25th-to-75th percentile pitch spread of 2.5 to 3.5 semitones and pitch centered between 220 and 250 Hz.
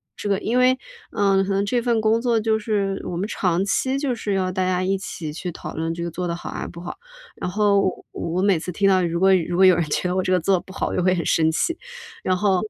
No: average, 2.8 semitones; high, 190 Hz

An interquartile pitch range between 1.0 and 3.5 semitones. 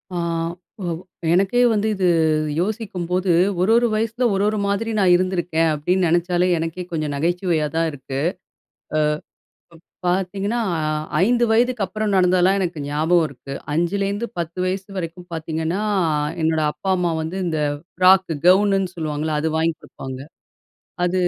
Yes: average, 3.2 semitones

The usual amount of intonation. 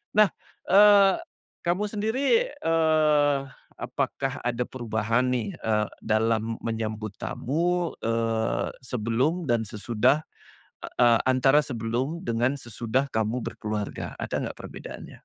No: wide, 5.8 semitones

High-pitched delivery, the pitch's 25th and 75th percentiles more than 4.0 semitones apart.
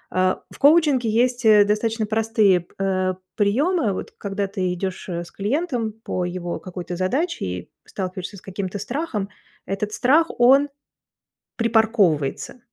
Yes: high, 205 Hz; average, 4.6 semitones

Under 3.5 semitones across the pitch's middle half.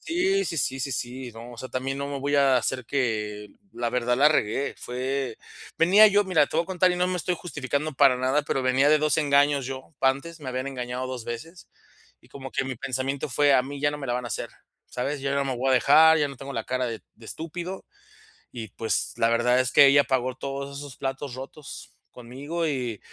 Yes: average, 2.7 semitones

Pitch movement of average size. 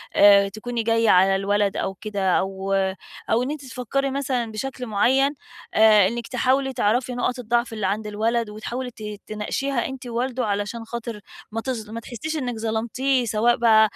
Yes: average, 3.0 semitones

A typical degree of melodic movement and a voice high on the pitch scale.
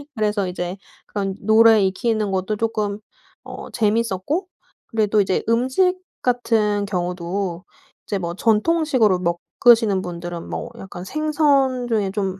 Yes: average, 3.8 semitones; high, 210 Hz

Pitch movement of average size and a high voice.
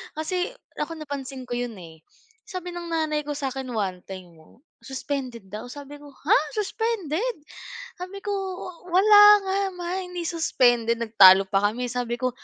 No: wide, 7.1 semitones; very high, 280 Hz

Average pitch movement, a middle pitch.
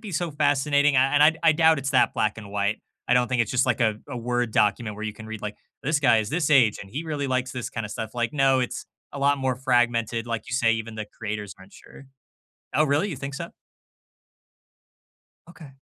No: average, 4.4 semitones; low, 125 Hz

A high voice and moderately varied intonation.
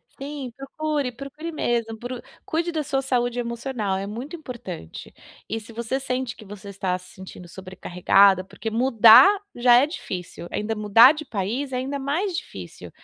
Yes: high, 240 Hz; average, 4.9 semitones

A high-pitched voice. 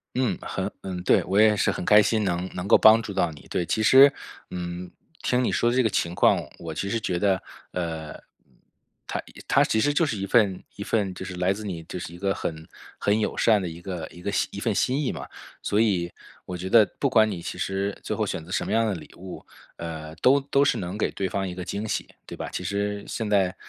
No: low, 100 Hz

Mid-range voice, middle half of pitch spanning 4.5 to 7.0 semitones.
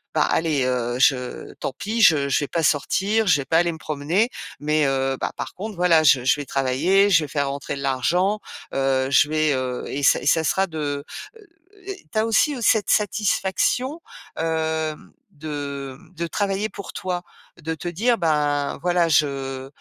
Yes: medium, 155 Hz; wide, 5.4 semitones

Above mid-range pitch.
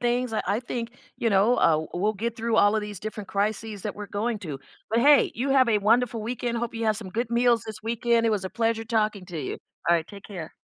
Yes: high, 220 Hz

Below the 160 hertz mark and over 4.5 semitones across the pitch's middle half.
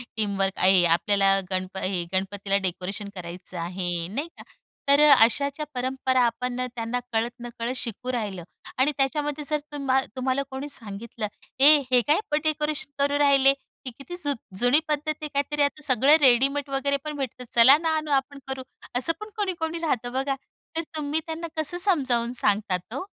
No: very high, 260 Hz; average, 5.0 semitones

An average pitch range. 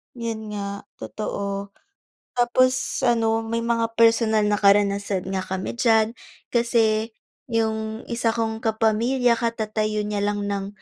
No: narrow, 1.9 semitones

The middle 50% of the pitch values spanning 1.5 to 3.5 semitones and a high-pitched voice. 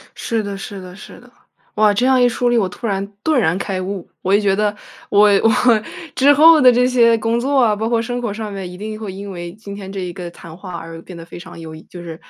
No: average, 4.0 semitones; high, 205 Hz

